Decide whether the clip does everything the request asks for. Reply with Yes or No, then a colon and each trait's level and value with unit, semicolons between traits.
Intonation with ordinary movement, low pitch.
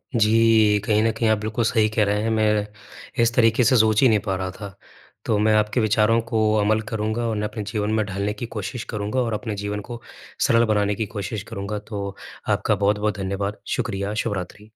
No: narrow, 1.5 semitones; low, 105 Hz